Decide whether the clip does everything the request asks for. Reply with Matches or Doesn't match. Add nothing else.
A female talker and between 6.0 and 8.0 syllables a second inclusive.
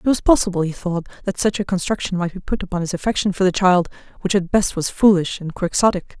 Matches